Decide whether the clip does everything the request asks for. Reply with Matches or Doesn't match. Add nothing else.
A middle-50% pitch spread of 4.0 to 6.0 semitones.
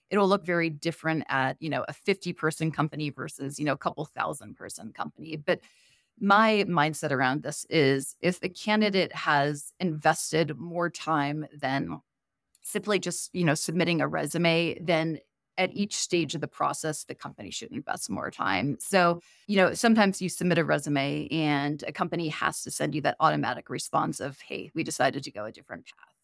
Doesn't match